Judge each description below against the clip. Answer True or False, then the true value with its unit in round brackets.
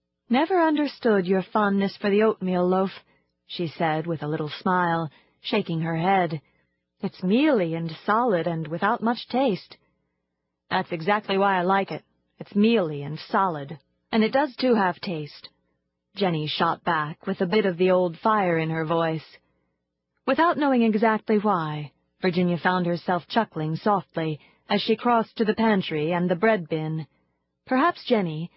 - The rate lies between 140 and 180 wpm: True (160 wpm)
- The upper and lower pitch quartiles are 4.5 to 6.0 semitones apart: True (5.3 semitones)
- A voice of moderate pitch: True (180 Hz)